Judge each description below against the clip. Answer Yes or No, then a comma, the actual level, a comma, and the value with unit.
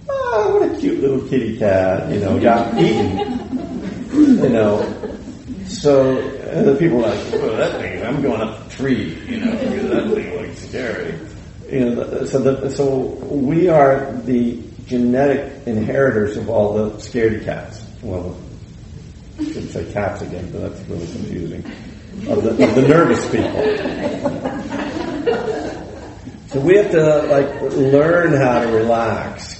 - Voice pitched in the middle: No, low, 125 Hz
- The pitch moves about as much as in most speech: No, wide, 5.7 semitones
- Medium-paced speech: Yes, average, 150 wpm